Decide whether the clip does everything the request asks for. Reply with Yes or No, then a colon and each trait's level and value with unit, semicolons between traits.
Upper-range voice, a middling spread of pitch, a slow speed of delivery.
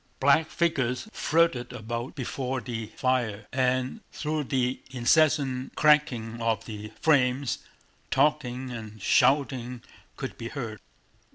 No: low, 125 Hz; average, 3.2 semitones; slow, 110 wpm